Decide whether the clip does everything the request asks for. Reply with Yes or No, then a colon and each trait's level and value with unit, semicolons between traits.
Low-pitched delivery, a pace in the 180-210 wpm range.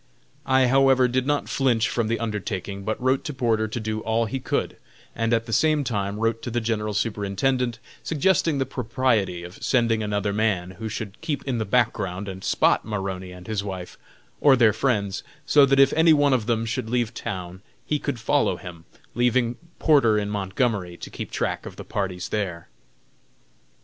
Yes: low, 115 Hz; average, 185 wpm